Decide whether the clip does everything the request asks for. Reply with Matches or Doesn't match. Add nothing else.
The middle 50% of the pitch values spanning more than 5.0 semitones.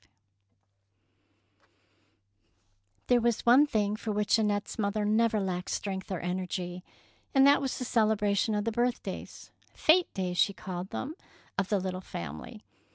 Doesn't match